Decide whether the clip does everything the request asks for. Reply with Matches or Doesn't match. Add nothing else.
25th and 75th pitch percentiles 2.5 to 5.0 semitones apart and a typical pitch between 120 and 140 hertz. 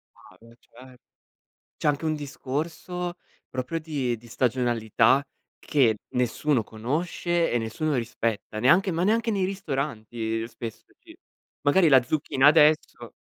Doesn't match